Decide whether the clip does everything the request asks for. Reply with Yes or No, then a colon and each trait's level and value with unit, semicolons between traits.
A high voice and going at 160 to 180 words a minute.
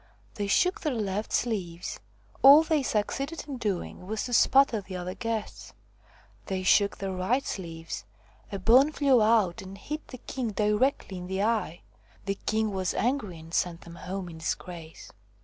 Yes: high, 205 Hz; average, 165 wpm